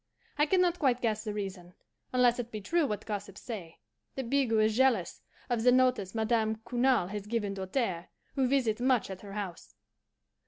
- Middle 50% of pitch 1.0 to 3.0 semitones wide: No, average, 3.8 semitones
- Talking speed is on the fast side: No, average, 185 wpm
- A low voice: No, high, 225 Hz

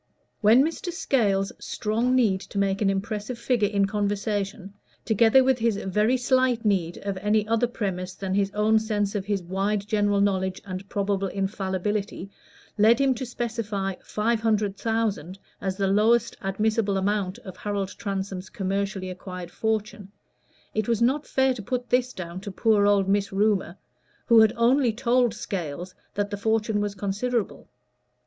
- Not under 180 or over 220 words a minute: No, average, 160 wpm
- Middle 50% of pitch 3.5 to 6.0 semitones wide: No, average, 2.7 semitones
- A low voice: No, high, 205 Hz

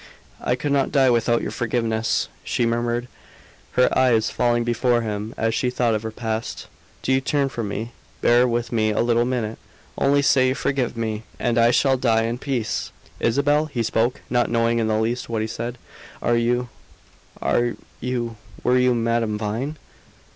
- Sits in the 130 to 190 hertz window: No, low, 120 Hz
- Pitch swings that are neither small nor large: No, narrow, 1.8 semitones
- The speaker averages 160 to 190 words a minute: Yes, average, 180 wpm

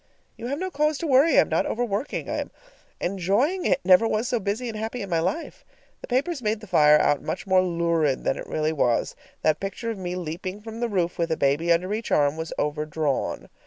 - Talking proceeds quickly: Yes, fast, 230 wpm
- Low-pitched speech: No, high, 190 Hz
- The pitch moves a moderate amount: No, wide, 6.2 semitones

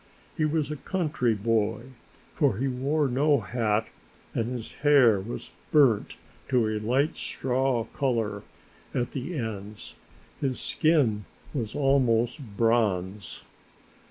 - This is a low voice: Yes, low, 120 Hz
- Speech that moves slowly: Yes, slow, 120 wpm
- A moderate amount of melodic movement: Yes, average, 4.1 semitones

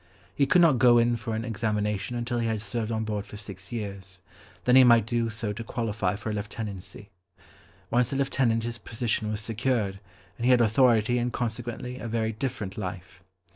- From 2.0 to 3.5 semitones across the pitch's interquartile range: Yes, narrow, 2.4 semitones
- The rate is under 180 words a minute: No, average, 195 wpm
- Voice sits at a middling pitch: No, low, 115 Hz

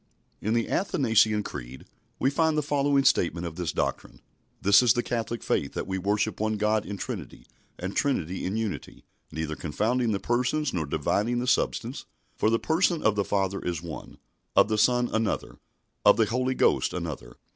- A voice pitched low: Yes, low, 110 Hz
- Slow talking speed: No, average, 180 wpm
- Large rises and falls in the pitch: No, average, 4.8 semitones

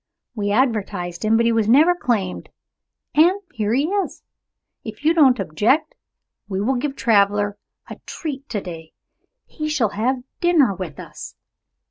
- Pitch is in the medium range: No, high, 230 Hz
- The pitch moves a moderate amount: No, wide, 5.9 semitones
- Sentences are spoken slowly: No, average, 150 wpm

